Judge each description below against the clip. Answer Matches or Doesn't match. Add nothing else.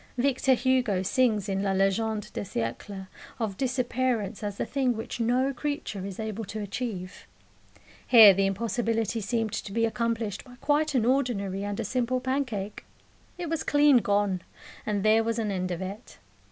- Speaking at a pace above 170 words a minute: Doesn't match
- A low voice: Doesn't match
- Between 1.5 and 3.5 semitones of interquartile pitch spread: Doesn't match